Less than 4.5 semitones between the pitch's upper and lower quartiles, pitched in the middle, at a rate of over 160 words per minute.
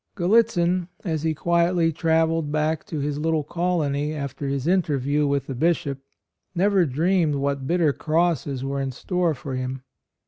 No: average, 3.5 semitones; medium, 155 Hz; average, 150 wpm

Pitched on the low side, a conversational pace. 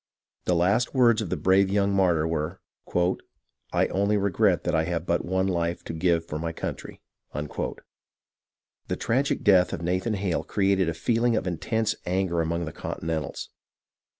Yes: very low, 90 Hz; average, 170 wpm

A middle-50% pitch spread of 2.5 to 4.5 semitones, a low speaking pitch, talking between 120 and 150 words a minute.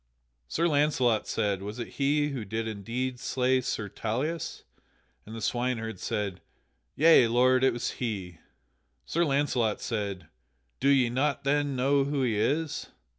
Yes: average, 4.0 semitones; low, 125 Hz; average, 145 wpm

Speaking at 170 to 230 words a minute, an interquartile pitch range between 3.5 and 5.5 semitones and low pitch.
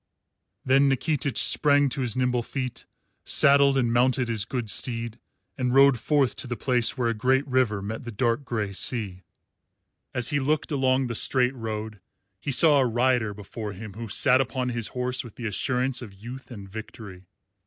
No: average, 180 wpm; average, 3.0 semitones; low, 125 Hz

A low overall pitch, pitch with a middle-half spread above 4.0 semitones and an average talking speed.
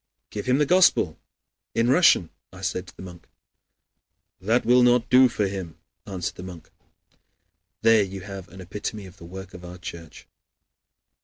Yes: very low, 95 Hz; average, 4.4 semitones; average, 165 wpm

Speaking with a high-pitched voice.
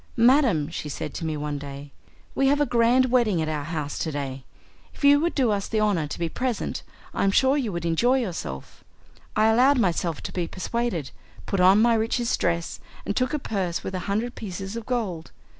Yes: high, 200 Hz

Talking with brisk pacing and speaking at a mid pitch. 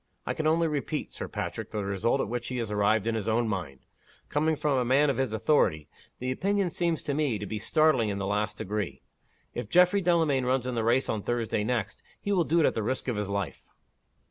No: fast, 235 wpm; low, 120 Hz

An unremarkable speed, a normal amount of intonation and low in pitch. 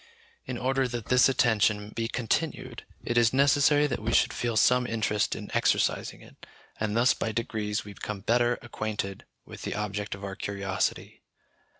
Yes: average, 170 wpm; average, 3.0 semitones; low, 115 Hz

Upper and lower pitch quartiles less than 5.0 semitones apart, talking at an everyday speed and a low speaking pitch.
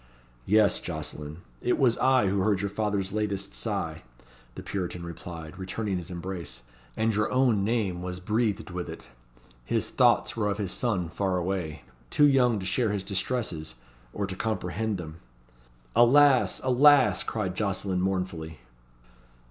Yes: average, 3.6 semitones; average, 150 wpm; low, 100 Hz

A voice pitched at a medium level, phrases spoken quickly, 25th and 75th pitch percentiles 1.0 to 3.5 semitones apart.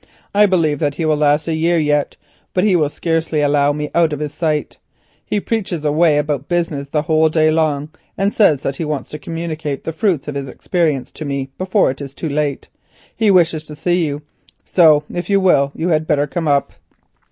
Yes: medium, 155 Hz; fast, 210 wpm; narrow, 2.6 semitones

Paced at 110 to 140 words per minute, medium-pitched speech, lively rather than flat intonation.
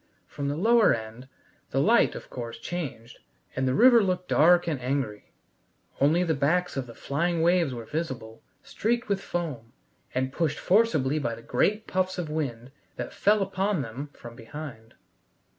No: average, 165 wpm; medium, 150 Hz; wide, 6.2 semitones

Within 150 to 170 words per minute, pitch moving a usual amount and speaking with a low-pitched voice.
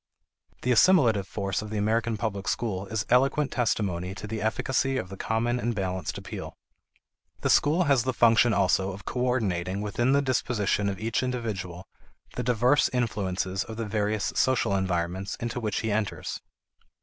Yes: average, 160 wpm; average, 3.9 semitones; low, 110 Hz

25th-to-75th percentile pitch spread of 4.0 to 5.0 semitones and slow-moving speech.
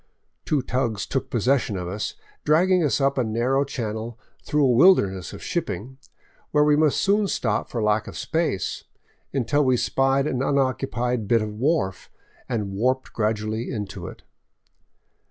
No: average, 4.4 semitones; average, 155 wpm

